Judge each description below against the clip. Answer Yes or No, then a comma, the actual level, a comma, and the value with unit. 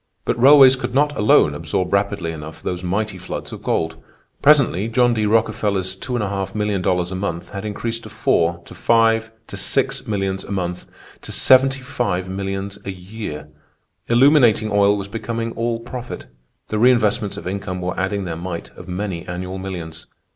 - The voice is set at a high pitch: No, low, 100 Hz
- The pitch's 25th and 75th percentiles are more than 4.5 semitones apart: No, average, 3.8 semitones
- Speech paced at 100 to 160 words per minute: Yes, average, 155 wpm